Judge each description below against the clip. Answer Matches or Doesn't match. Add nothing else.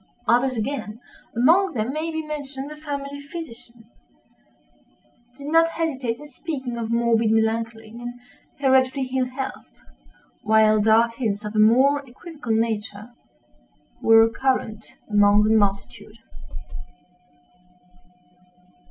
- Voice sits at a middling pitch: Doesn't match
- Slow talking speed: Matches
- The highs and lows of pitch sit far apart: Doesn't match